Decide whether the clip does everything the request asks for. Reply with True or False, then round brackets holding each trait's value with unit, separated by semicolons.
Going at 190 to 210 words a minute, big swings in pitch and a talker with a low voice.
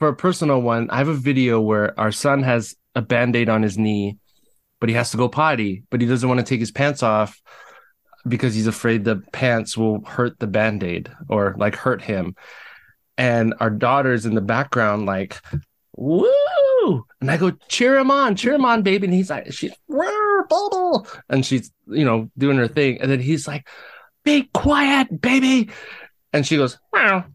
True (195 wpm; 6.3 semitones; 125 Hz)